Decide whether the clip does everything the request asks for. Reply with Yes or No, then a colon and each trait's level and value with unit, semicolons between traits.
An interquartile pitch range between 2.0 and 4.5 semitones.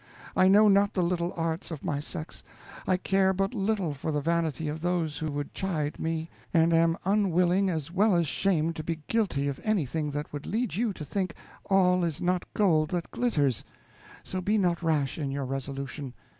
Yes: average, 4.0 semitones